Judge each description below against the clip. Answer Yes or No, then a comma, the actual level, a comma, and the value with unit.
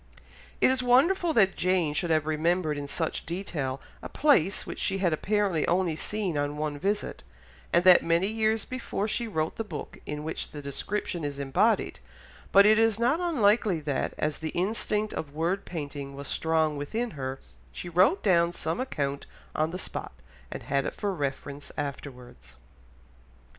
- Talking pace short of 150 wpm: No, average, 175 wpm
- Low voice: No, medium, 170 Hz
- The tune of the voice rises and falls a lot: Yes, wide, 6.0 semitones